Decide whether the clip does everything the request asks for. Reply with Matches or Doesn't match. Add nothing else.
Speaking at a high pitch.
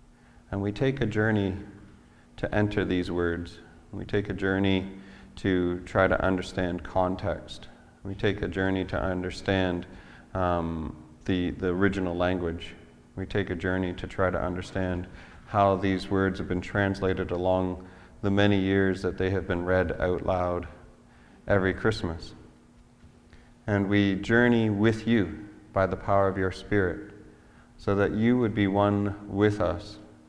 Doesn't match